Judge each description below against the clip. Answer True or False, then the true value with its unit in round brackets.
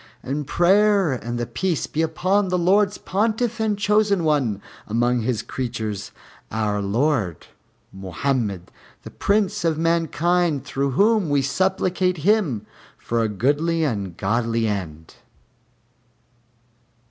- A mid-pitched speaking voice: True (145 Hz)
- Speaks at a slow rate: True (125 wpm)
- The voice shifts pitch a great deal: True (8.5 semitones)